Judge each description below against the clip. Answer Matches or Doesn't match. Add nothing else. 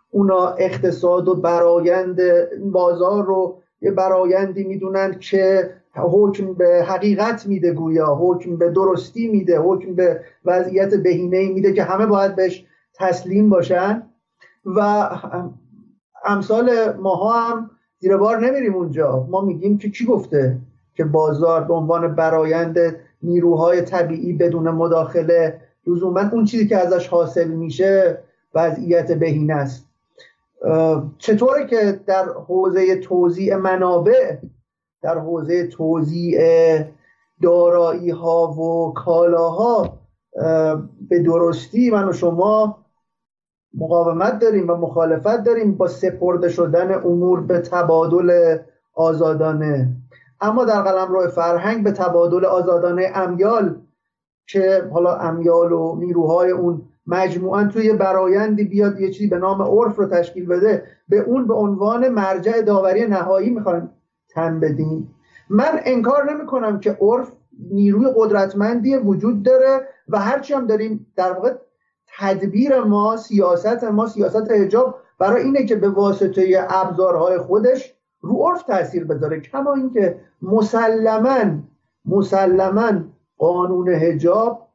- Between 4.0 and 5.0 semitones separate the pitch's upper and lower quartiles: Doesn't match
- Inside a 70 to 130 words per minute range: Matches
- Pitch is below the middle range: Doesn't match